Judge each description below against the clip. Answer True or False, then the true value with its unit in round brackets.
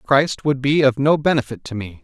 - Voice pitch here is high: False (135 Hz)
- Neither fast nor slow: False (235 wpm)